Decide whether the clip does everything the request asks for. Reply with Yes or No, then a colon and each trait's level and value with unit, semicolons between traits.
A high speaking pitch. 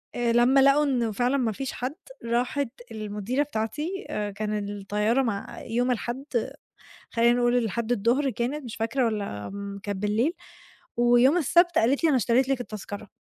Yes: high, 240 Hz